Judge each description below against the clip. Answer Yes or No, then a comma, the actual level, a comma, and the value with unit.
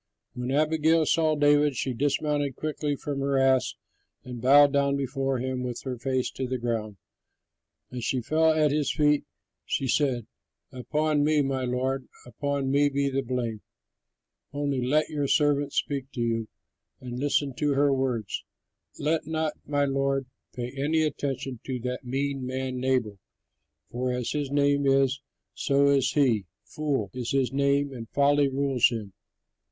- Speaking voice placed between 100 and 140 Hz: Yes, low, 135 Hz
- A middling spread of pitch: No, narrow, 2.3 semitones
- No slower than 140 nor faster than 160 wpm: Yes, average, 155 wpm